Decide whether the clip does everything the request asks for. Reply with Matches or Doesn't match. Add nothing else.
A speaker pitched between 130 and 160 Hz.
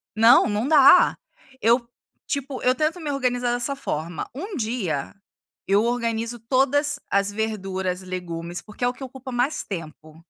Doesn't match